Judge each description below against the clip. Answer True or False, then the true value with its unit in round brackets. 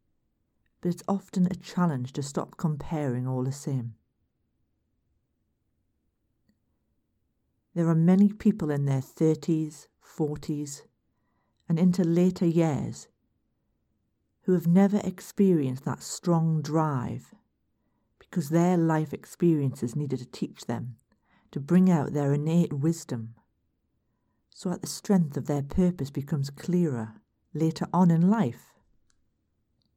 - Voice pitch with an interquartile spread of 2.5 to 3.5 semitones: False (5.2 semitones)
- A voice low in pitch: False (155 Hz)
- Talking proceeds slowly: True (115 wpm)